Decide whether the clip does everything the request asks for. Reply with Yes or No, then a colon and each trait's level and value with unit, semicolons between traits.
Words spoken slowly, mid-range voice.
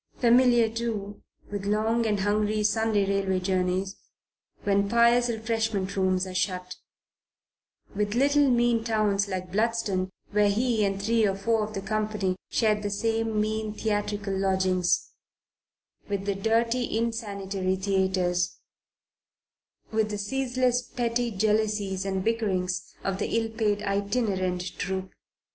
No: slow, 125 wpm; high, 210 Hz